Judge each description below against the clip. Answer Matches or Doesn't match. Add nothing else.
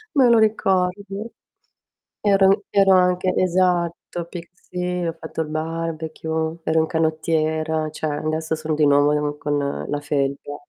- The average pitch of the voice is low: Doesn't match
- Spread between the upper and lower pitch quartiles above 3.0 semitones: Doesn't match